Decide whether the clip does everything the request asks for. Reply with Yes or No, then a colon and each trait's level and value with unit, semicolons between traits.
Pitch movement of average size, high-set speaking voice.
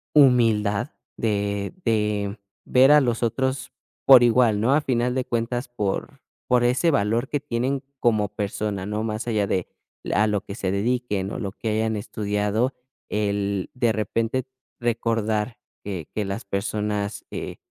No: average, 3.0 semitones; low, 110 Hz